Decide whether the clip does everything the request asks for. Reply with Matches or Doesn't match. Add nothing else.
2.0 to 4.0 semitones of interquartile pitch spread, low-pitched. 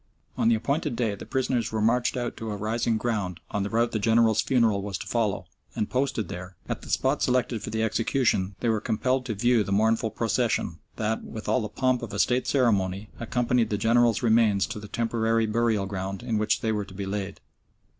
Matches